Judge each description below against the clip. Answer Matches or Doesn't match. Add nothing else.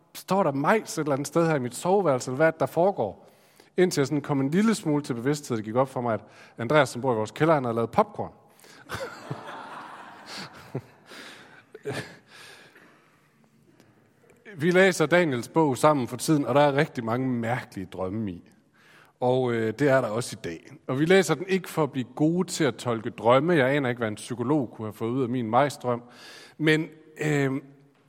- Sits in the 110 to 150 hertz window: Matches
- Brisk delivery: Doesn't match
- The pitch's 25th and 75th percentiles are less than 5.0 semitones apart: Matches